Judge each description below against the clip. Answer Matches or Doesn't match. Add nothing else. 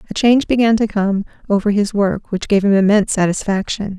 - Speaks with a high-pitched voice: Matches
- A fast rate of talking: Doesn't match